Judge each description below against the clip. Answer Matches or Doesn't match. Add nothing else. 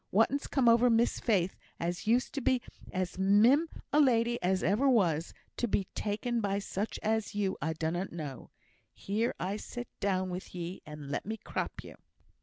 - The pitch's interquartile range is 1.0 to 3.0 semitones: Doesn't match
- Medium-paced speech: Matches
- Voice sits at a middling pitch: Doesn't match